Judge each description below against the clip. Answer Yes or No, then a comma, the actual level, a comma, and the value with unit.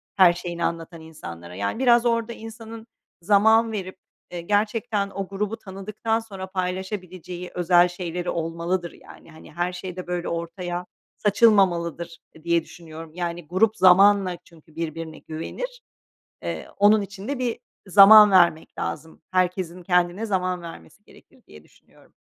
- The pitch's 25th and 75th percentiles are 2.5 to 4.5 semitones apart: Yes, average, 3.3 semitones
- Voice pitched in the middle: Yes, medium, 180 Hz